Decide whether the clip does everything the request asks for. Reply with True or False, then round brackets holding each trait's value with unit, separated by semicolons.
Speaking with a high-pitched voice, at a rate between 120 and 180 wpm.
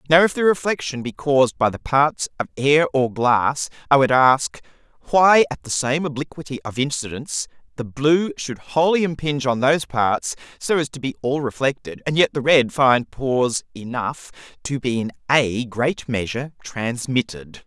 False (135 Hz; 175 wpm)